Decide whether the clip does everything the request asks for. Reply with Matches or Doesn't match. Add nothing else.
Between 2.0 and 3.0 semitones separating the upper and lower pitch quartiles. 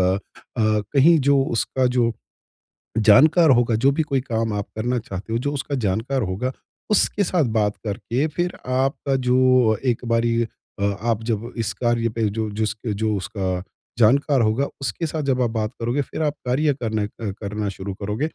Doesn't match